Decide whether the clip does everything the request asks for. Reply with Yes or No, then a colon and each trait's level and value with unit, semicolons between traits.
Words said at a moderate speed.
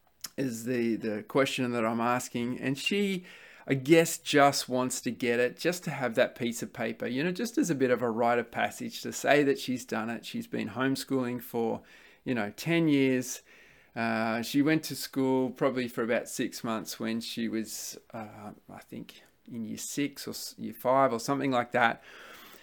Yes: average, 195 wpm